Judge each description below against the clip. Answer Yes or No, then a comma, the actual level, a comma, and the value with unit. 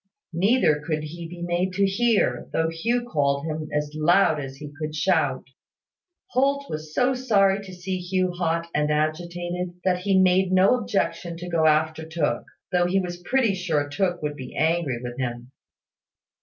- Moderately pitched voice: Yes, medium, 175 Hz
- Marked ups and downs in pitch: No, average, 3.6 semitones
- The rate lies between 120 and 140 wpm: No, average, 170 wpm